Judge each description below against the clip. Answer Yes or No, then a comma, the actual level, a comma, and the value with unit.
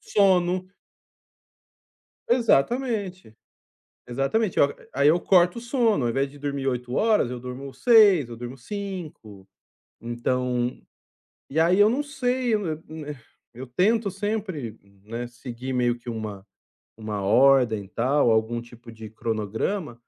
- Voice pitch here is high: No, low, 135 Hz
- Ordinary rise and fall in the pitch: No, wide, 8.5 semitones